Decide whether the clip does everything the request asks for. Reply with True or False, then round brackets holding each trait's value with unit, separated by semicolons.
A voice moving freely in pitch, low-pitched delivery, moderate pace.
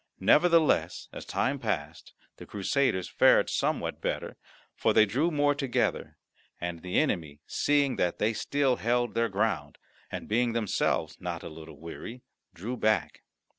True (7.2 semitones; 110 Hz; 145 wpm)